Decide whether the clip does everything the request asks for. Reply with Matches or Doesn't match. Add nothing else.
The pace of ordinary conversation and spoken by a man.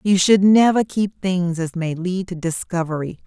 Doesn't match